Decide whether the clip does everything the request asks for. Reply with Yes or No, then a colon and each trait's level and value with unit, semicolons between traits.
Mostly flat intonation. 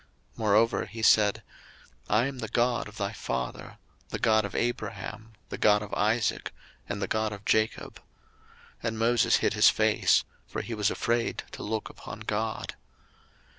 Yes: narrow, 1.7 semitones